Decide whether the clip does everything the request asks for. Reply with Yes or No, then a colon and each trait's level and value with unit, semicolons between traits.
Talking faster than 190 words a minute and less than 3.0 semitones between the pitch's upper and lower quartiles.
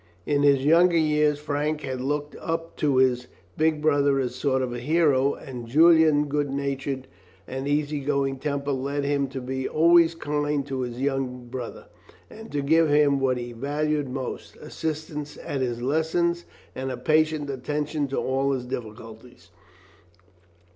No: average, 160 wpm; narrow, 2.5 semitones